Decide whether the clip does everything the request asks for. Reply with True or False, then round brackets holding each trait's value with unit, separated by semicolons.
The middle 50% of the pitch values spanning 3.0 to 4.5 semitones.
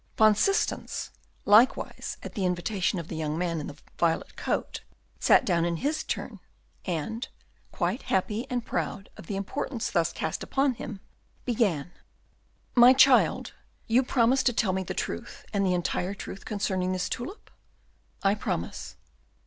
False (5.4 semitones)